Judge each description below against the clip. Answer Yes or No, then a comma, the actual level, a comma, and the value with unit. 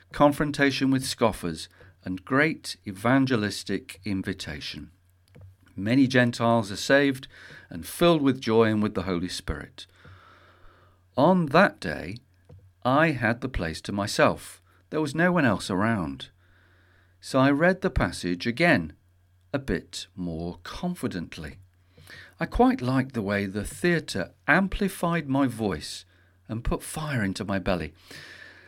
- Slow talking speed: Yes, slow, 130 wpm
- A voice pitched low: Yes, low, 100 Hz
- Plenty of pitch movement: Yes, wide, 6.6 semitones